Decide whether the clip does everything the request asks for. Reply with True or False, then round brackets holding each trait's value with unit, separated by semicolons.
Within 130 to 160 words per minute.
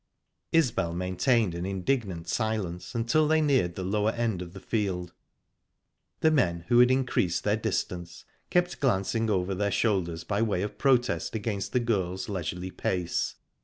True (155 wpm)